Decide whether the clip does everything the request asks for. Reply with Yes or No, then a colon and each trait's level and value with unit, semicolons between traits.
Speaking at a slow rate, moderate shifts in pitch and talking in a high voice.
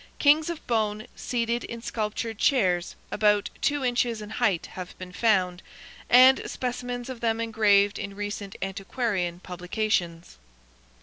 Yes: slow, 130 wpm; average, 3.8 semitones; high, 215 Hz